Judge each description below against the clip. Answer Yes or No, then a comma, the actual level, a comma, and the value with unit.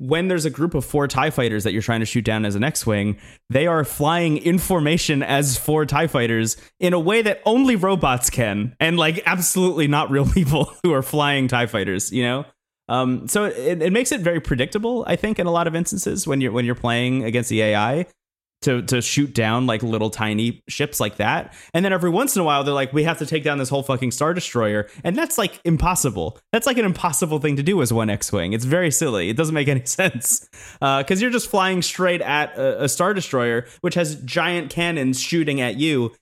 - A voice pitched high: No, medium, 145 Hz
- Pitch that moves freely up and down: Yes, wide, 6.0 semitones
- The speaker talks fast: Yes, fast, 230 wpm